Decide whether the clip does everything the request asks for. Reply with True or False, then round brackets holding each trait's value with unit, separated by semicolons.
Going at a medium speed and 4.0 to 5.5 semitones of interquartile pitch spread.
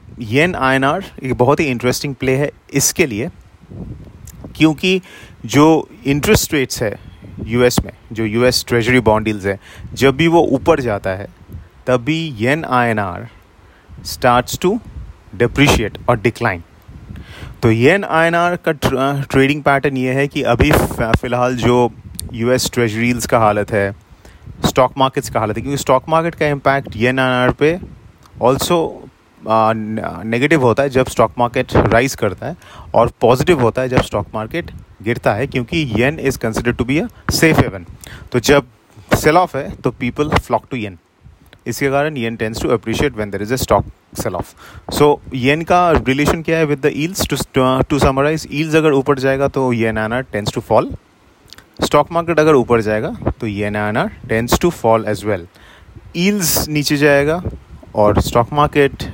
True (175 wpm; 4.7 semitones)